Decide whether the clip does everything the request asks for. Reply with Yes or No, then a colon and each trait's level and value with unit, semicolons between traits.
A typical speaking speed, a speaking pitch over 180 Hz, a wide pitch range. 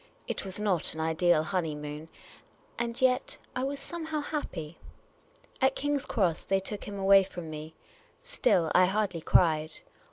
Yes: average, 150 wpm; high, 190 Hz; wide, 7.7 semitones